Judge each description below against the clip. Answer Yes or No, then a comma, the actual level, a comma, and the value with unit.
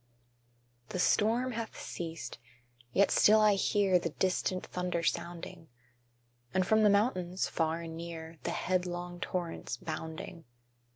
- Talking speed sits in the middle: No, slow, 130 wpm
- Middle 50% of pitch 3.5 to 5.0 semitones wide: No, average, 3.0 semitones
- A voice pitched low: No, medium, 180 Hz